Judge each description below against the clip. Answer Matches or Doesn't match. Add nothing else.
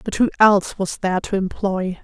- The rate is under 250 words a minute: Matches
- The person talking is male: Doesn't match